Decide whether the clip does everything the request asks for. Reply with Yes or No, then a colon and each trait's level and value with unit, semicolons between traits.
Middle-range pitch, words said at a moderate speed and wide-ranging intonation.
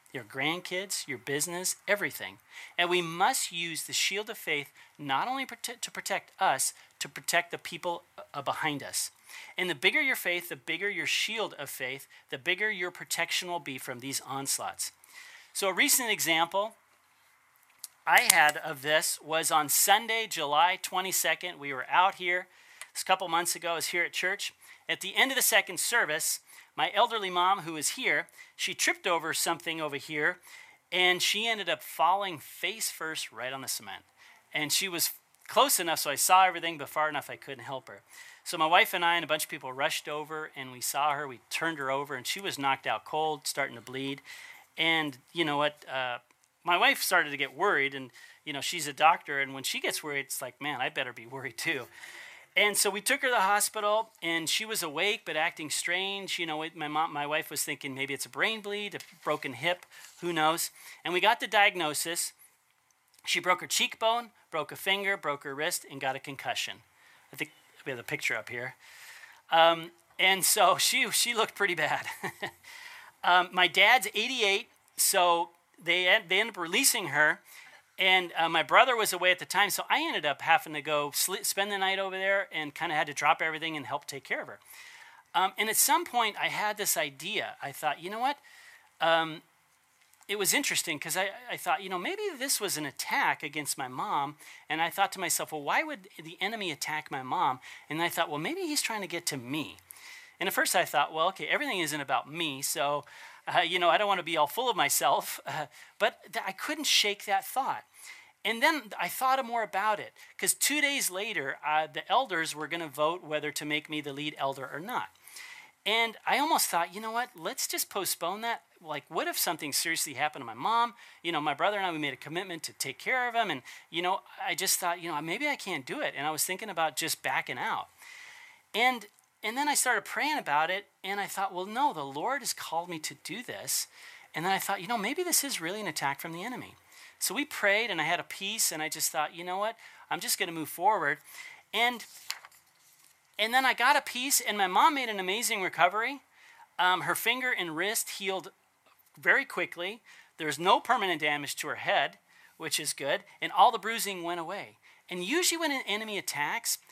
No: medium, 180 Hz; fast, 215 wpm; wide, 6.1 semitones